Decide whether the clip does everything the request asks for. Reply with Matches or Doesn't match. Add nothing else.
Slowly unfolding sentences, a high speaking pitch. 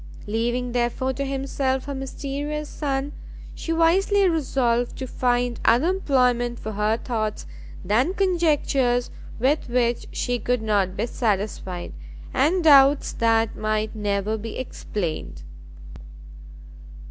Matches